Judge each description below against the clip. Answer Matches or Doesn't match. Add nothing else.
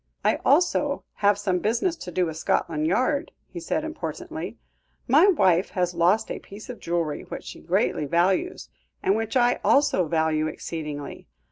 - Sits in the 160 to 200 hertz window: Matches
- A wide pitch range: Matches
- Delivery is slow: Doesn't match